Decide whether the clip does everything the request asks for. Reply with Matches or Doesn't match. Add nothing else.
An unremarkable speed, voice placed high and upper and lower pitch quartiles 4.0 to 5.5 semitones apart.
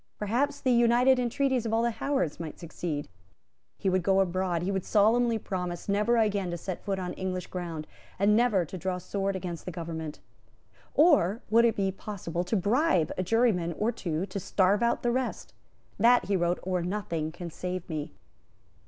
Matches